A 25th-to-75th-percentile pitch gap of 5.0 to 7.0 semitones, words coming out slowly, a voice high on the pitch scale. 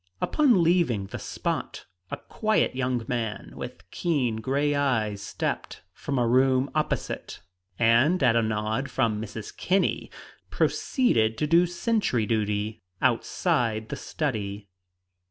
No: wide, 5.6 semitones; slow, 125 wpm; low, 125 Hz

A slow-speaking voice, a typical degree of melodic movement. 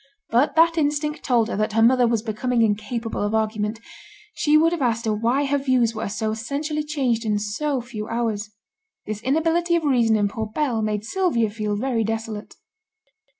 No: average, 185 wpm; average, 4.8 semitones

